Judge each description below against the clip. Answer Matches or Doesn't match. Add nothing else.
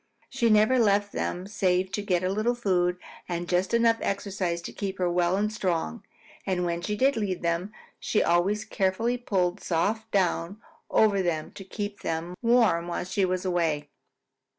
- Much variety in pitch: Doesn't match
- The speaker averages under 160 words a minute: Doesn't match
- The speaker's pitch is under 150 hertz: Doesn't match